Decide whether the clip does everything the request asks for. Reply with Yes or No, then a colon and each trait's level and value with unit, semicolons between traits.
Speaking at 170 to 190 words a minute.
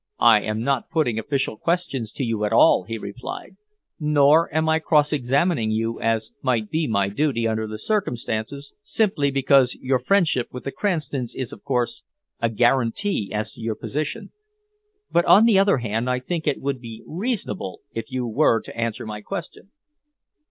Yes: average, 175 wpm